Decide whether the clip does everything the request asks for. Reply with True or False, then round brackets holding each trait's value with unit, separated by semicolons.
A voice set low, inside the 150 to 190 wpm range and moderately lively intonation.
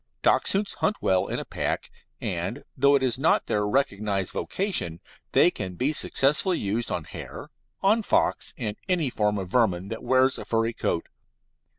False (115 Hz; 170 wpm; 6.0 semitones)